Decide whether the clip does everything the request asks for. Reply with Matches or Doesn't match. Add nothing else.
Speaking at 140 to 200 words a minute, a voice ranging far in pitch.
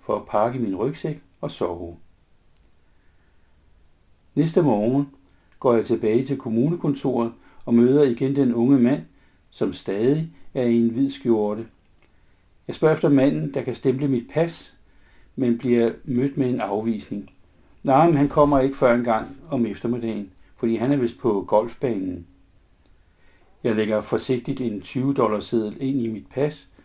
Matches